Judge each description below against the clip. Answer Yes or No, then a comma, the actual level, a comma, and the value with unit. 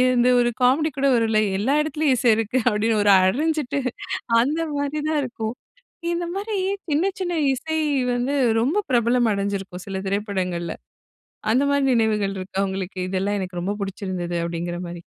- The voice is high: Yes, high, 225 Hz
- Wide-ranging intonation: Yes, wide, 6.5 semitones